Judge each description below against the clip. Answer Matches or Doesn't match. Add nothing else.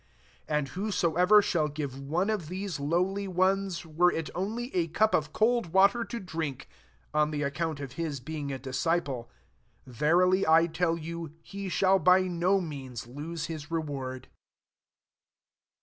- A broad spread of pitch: Doesn't match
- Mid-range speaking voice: Matches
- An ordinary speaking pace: Matches